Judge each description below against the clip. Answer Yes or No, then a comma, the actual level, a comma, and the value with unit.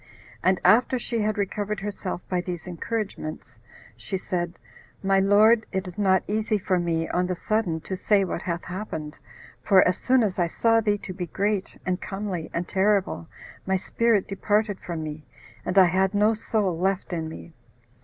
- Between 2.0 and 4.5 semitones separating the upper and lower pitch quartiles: Yes, average, 2.9 semitones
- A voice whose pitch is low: No, high, 190 Hz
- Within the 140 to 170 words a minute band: No, average, 180 wpm